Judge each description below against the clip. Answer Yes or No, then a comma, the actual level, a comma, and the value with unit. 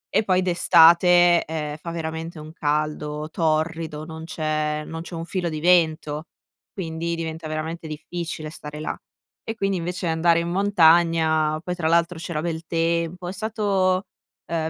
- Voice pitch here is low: No, medium, 165 Hz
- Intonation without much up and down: Yes, narrow, 1.9 semitones